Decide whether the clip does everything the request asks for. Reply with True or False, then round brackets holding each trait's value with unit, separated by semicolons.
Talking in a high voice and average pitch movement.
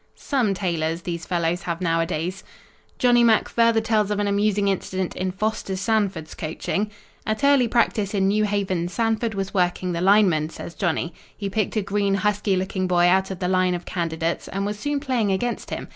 True (195 Hz; 3.3 semitones)